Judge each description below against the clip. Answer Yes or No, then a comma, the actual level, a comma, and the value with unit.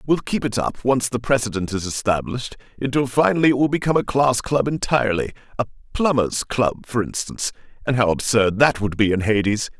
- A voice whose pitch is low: Yes, low, 120 Hz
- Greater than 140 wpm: Yes, average, 180 wpm